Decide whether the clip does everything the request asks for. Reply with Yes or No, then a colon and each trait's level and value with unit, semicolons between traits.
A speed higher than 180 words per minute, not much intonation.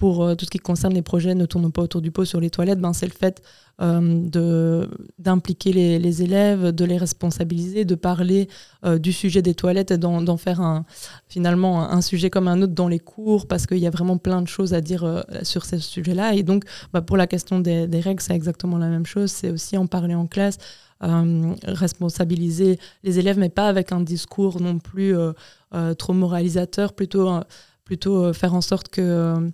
Yes: fast, 220 wpm; narrow, 1.6 semitones